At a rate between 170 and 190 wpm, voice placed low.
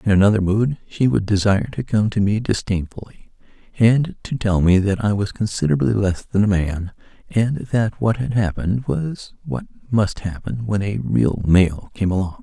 Yes: average, 185 wpm; low, 105 Hz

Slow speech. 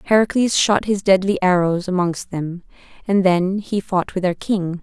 No: average, 175 wpm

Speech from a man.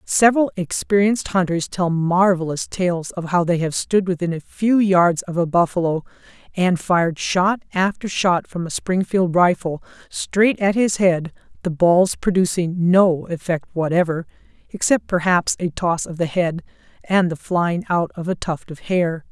No: female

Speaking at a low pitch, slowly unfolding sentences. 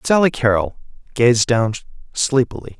Yes: low, 120 Hz; slow, 105 wpm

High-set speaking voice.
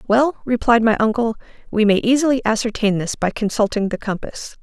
Yes: high, 225 Hz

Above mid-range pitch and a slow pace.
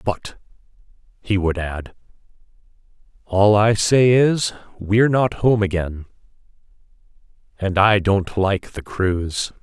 No: low, 100 Hz; slow, 110 wpm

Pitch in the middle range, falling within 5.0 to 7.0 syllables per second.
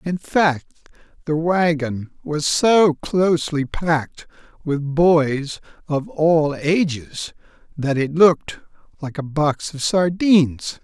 No: medium, 155 Hz; 3.4 syllables/s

